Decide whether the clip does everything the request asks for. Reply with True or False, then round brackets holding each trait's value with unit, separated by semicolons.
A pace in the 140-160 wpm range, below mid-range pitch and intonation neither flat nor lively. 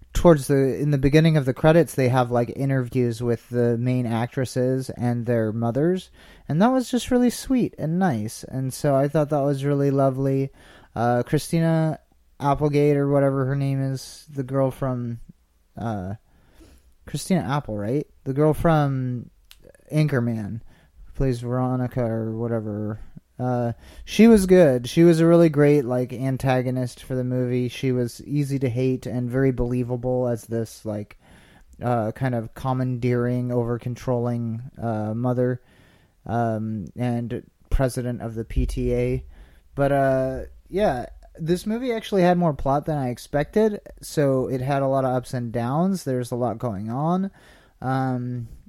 True (155 wpm; 130 Hz; 3.2 semitones)